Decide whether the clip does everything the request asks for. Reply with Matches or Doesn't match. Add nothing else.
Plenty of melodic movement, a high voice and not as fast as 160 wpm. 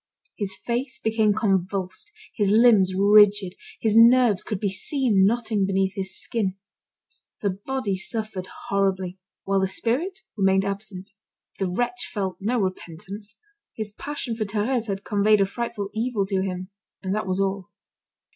Doesn't match